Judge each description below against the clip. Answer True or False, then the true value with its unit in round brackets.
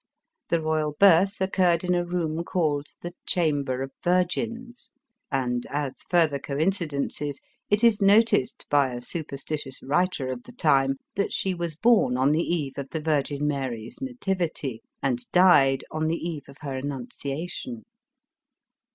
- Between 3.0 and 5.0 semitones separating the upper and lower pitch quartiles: True (4.7 semitones)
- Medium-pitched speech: True (155 Hz)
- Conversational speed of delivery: True (150 wpm)